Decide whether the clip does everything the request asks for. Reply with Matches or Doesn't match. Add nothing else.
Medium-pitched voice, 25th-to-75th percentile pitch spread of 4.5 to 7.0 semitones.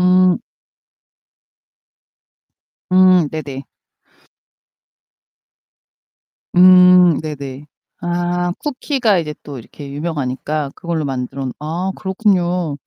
Doesn't match